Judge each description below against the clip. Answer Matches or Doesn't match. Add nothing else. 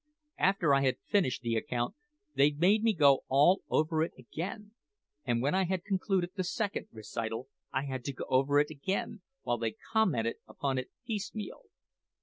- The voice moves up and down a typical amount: Doesn't match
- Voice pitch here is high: Doesn't match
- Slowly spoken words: Doesn't match